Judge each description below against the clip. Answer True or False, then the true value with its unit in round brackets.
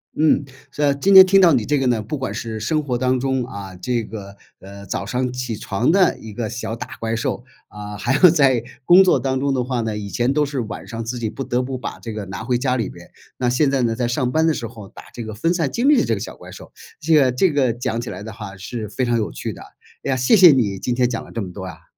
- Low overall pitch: True (125 Hz)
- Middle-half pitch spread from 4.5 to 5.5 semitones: False (3.8 semitones)